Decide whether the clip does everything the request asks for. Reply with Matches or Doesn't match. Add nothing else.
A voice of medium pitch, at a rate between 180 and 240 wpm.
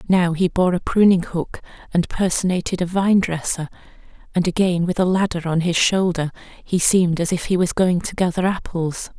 Matches